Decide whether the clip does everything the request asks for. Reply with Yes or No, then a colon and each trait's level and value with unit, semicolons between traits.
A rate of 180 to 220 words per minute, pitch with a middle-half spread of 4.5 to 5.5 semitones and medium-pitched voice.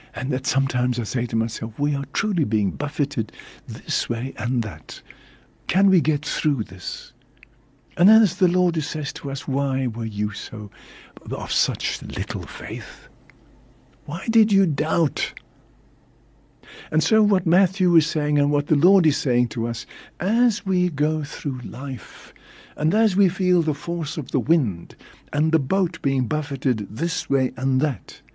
No: average, 165 wpm; average, 5.1 semitones; medium, 145 Hz